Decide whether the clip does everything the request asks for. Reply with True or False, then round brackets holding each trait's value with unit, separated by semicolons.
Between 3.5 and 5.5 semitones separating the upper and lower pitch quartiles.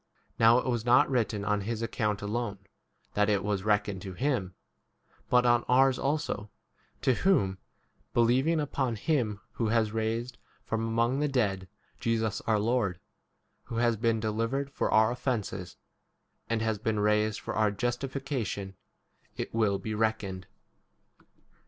False (3.0 semitones)